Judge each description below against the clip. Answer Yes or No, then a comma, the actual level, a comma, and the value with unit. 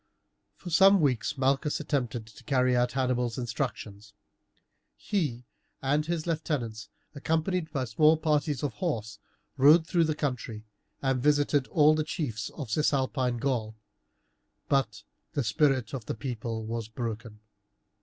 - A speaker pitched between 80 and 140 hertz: Yes, low, 135 Hz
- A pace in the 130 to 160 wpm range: Yes, slow, 135 wpm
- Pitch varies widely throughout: No, average, 4.6 semitones